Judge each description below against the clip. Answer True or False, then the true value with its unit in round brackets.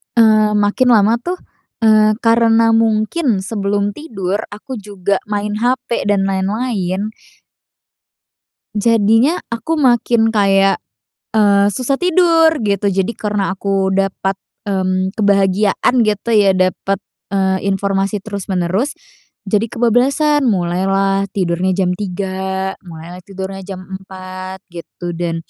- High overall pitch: True (200 Hz)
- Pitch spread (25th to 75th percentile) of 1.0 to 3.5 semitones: True (2.9 semitones)